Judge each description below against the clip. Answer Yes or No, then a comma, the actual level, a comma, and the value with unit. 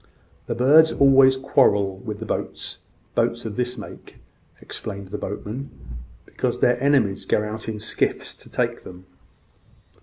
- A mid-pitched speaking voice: No, low, 110 Hz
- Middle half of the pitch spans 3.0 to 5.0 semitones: Yes, average, 4.3 semitones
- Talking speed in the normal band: Yes, average, 145 wpm